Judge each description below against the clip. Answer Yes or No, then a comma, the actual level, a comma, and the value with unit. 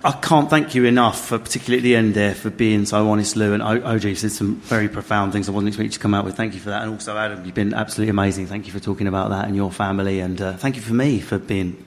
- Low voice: Yes, low, 105 Hz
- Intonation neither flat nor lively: No, narrow, 2.2 semitones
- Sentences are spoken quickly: Yes, fast, 295 wpm